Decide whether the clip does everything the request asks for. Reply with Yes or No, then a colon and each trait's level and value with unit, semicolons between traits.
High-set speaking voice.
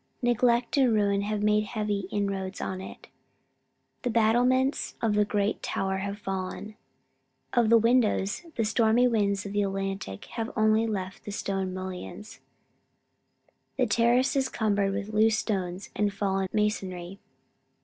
Yes: high, 210 Hz